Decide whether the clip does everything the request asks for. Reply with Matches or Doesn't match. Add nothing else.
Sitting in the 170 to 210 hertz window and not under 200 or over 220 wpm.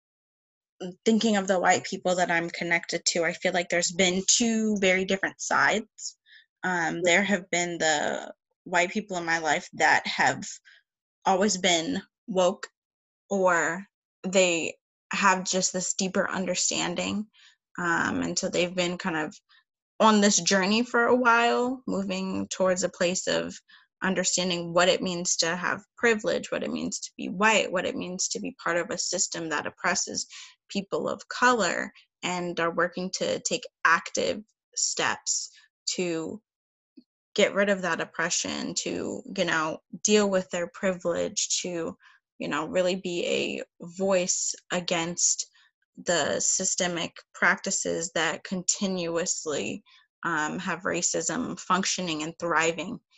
Doesn't match